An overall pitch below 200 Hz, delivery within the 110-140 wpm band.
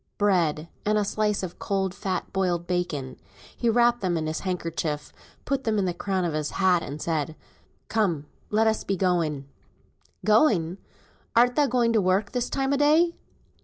No: high, 190 Hz; average, 170 wpm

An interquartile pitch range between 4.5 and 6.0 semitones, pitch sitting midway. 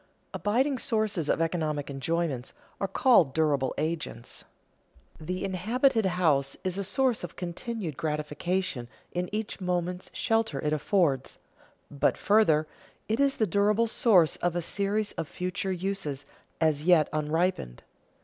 Yes: average, 5.1 semitones; medium, 180 Hz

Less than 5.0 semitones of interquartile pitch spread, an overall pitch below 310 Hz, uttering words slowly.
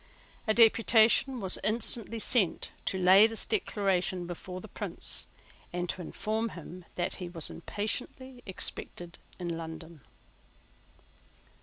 Yes: average, 4.2 semitones; high, 190 Hz; slow, 120 wpm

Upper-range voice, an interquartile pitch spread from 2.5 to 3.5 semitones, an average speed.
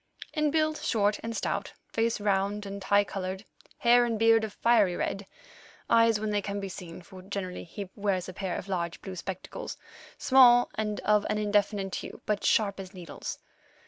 Yes: high, 205 Hz; average, 2.8 semitones; average, 175 wpm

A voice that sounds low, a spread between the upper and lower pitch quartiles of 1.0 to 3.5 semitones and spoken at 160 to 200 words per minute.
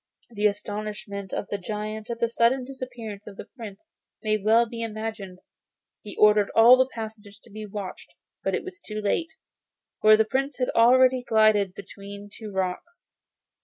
No: high, 215 Hz; narrow, 2.5 semitones; average, 165 wpm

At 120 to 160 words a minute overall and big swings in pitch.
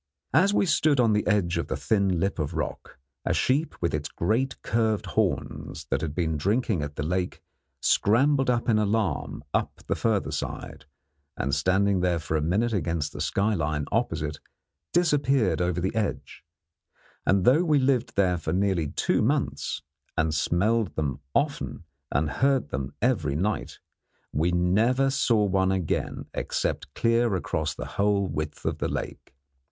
Yes: average, 155 wpm; wide, 6.2 semitones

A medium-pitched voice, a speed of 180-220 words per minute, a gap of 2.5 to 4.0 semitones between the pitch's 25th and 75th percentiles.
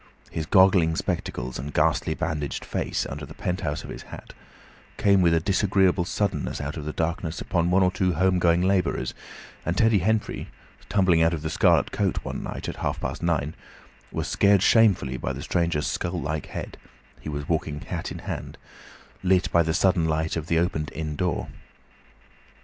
No: very low, 85 Hz; average, 185 wpm; average, 3.3 semitones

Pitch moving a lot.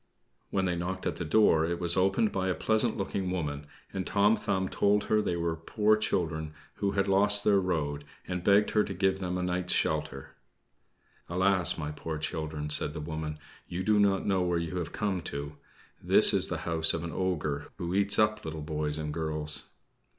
No: average, 3.8 semitones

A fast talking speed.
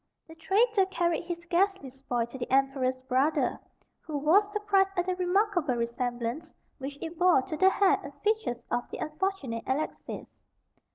No: average, 160 wpm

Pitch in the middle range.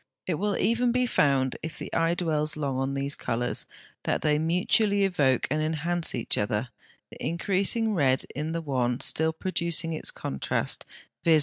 Yes: medium, 160 Hz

